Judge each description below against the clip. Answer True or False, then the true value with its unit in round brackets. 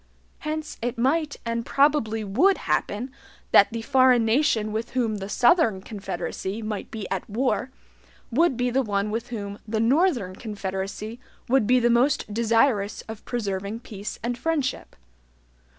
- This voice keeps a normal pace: True (150 wpm)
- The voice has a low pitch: False (230 Hz)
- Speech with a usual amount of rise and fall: True (3.6 semitones)